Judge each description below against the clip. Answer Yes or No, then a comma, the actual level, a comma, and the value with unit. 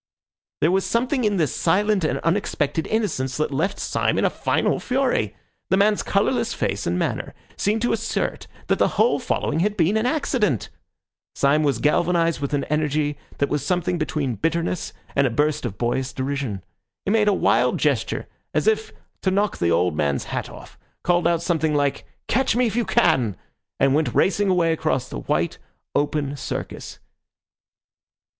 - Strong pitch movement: Yes, wide, 6.6 semitones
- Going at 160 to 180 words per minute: Yes, average, 175 wpm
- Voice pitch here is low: No, medium, 160 Hz